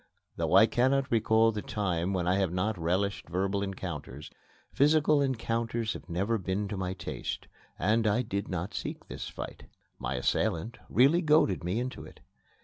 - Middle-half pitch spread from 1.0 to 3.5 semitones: No, average, 4.2 semitones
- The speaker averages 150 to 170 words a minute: Yes, average, 165 wpm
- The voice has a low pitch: Yes, low, 100 Hz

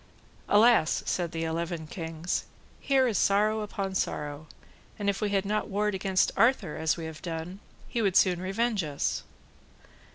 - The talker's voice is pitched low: No, high, 190 Hz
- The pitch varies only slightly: No, average, 4.2 semitones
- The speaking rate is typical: Yes, average, 160 wpm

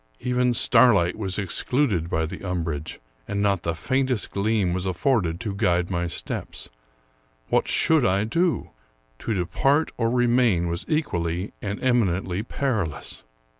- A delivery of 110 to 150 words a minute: Yes, average, 145 wpm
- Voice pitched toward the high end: No, low, 100 Hz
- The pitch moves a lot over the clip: Yes, wide, 5.9 semitones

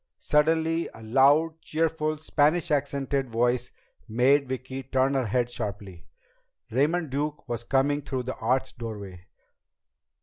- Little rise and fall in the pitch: No, average, 3.7 semitones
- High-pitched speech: No, low, 135 Hz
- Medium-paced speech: No, slow, 125 wpm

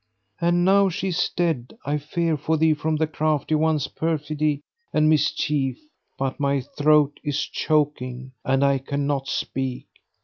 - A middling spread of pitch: No, narrow, 2.2 semitones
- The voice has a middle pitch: Yes, medium, 150 Hz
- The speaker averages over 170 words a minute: No, average, 145 wpm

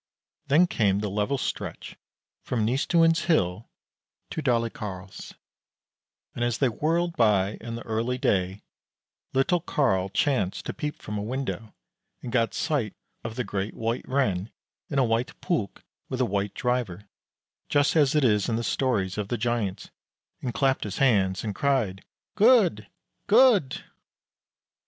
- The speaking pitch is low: Yes, low, 120 Hz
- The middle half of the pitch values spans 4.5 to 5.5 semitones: Yes, average, 5.0 semitones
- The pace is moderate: Yes, average, 145 wpm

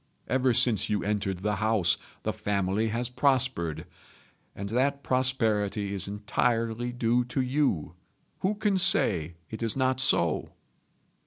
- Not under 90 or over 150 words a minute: Yes, slow, 135 wpm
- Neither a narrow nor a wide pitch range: Yes, average, 4.3 semitones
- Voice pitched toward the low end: Yes, low, 115 Hz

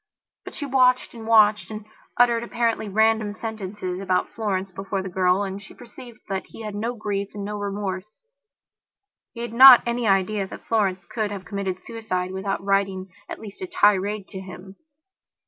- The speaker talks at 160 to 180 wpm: Yes, average, 175 wpm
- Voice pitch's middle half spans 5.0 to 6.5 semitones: No, average, 2.7 semitones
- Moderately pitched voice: No, high, 205 Hz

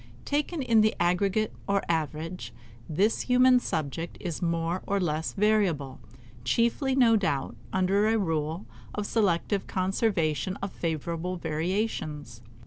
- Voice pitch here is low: No, medium, 185 Hz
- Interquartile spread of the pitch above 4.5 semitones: Yes, average, 5.0 semitones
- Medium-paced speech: No, slow, 125 wpm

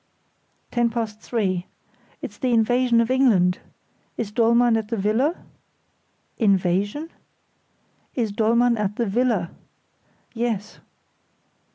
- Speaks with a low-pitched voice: No, high, 225 Hz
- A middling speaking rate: No, slow, 100 wpm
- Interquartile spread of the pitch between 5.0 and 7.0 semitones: No, average, 2.8 semitones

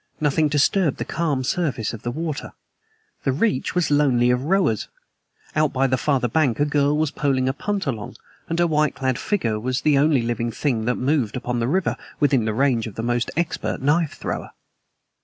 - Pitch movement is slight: No, average, 4.1 semitones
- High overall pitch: No, medium, 140 Hz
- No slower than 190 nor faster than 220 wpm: Yes, average, 195 wpm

